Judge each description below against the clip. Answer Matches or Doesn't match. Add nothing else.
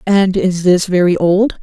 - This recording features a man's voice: Doesn't match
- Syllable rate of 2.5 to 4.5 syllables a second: Matches